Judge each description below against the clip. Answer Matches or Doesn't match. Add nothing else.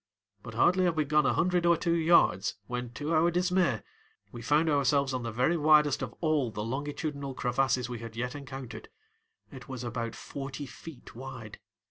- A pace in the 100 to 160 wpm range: Doesn't match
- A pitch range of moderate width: Matches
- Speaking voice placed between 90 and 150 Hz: Matches